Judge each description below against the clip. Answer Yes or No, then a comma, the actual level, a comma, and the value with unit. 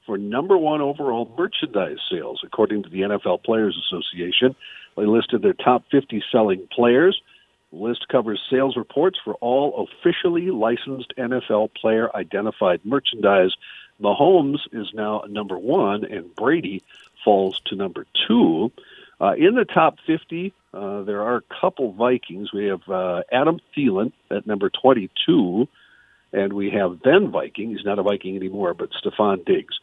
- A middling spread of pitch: No, wide, 7.1 semitones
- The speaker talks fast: No, average, 150 wpm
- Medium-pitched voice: No, low, 115 Hz